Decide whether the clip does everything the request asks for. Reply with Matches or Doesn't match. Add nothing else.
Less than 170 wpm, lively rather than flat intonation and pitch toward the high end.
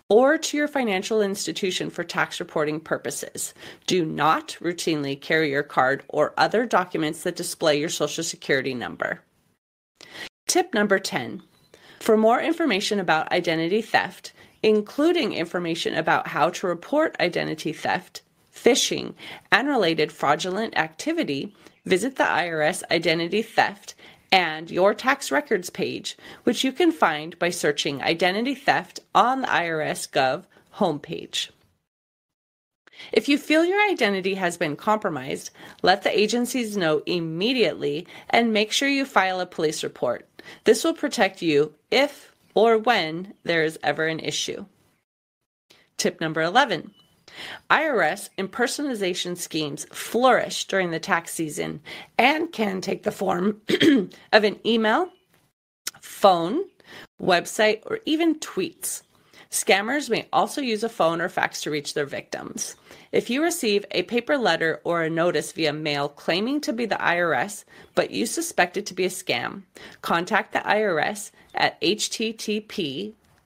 Matches